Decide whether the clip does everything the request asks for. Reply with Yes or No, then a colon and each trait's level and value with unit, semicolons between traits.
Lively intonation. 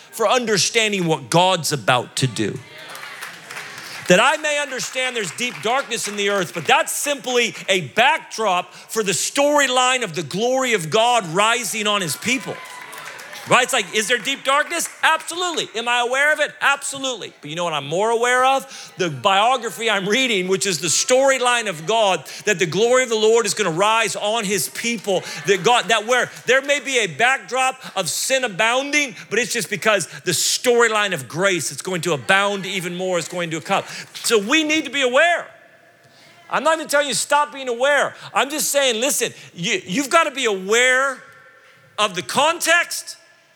Yes: wide, 5.9 semitones